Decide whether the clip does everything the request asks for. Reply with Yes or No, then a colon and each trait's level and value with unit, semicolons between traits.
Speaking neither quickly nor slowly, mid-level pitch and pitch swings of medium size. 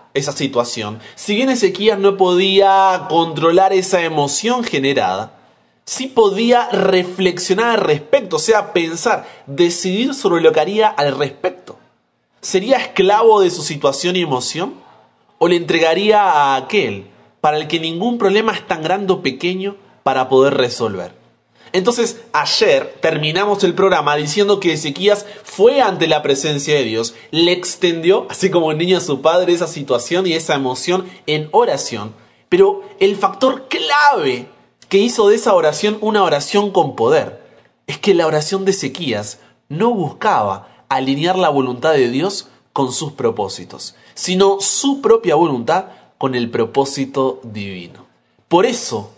No: average, 150 wpm; medium, 180 Hz; wide, 5.9 semitones